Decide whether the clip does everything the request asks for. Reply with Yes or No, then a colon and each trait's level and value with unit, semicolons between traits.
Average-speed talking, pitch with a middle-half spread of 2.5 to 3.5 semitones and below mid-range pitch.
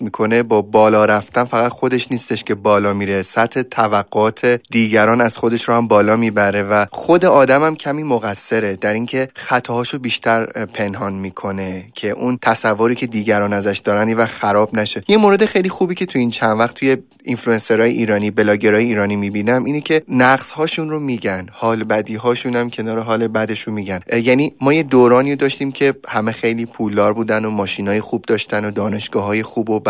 No: fast, 180 wpm; average, 3.1 semitones; low, 115 Hz